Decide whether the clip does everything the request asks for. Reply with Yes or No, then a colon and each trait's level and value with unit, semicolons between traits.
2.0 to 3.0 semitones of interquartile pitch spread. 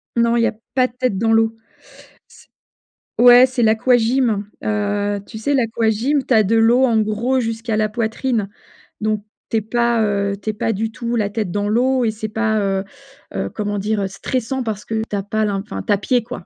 Yes: narrow, 2.5 semitones